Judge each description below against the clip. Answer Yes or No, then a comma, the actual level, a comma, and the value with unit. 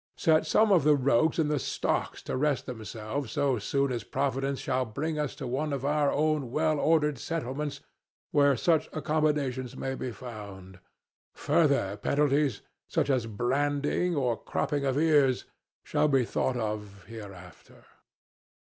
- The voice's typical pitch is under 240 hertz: Yes, medium, 140 Hz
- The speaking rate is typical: Yes, average, 150 wpm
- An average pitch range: Yes, average, 3.6 semitones